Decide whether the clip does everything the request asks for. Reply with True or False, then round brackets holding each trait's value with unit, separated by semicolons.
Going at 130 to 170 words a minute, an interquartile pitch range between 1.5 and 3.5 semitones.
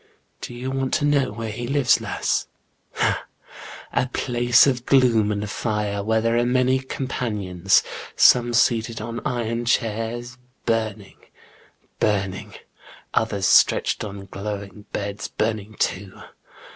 True (140 wpm; 2.9 semitones)